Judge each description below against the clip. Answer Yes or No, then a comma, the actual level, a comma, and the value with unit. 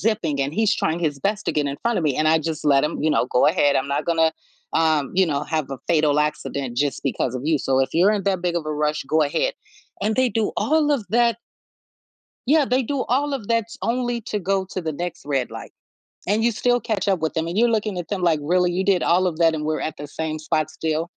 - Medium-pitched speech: Yes, medium, 165 Hz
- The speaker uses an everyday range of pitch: No, wide, 5.8 semitones